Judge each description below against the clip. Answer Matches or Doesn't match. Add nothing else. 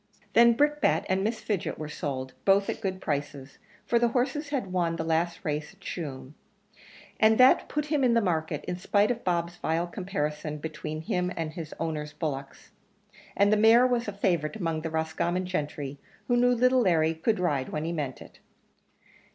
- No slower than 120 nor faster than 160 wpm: Doesn't match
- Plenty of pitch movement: Matches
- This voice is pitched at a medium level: Matches